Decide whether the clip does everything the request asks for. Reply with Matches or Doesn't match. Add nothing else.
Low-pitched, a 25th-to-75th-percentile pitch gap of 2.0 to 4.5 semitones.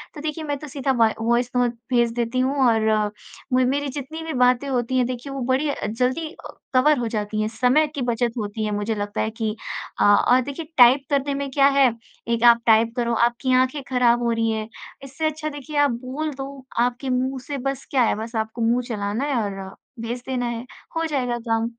Doesn't match